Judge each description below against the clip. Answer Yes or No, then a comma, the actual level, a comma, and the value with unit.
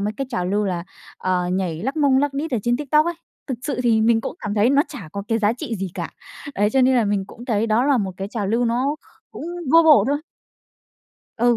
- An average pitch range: Yes, average, 5.0 semitones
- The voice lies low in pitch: No, high, 235 Hz